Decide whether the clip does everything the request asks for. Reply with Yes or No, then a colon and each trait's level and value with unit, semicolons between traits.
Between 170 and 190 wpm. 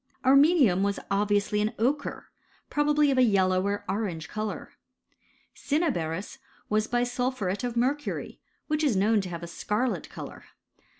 No: average, 155 wpm